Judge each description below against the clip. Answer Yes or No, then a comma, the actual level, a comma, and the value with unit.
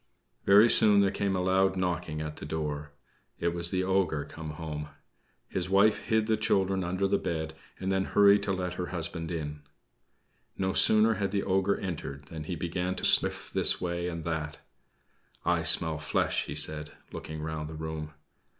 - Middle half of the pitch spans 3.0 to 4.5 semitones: Yes, average, 3.5 semitones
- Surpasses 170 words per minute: Yes, average, 180 wpm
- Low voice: Yes, very low, 90 Hz